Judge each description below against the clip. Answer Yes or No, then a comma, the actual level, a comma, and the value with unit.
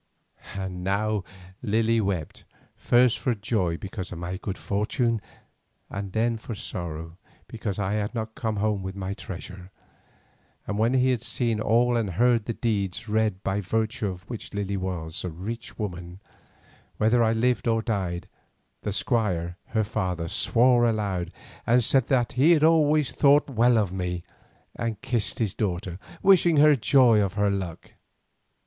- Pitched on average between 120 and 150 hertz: No, low, 105 Hz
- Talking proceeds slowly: No, average, 155 wpm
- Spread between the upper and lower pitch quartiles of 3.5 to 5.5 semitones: Yes, average, 3.9 semitones